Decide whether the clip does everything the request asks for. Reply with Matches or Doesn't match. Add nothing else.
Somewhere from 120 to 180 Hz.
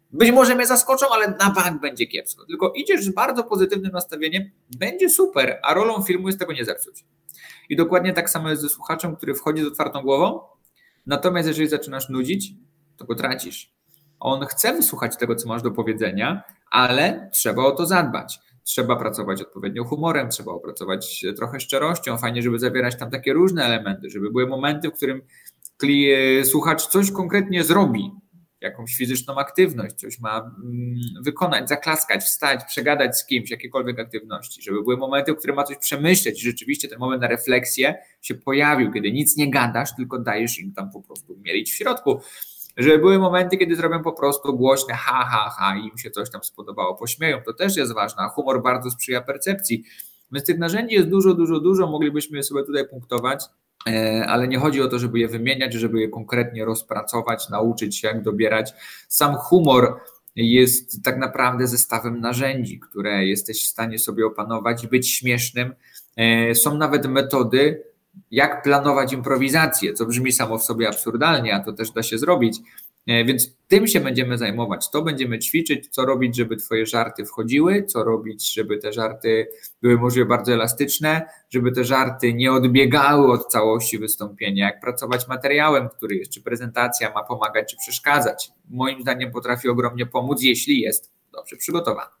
Matches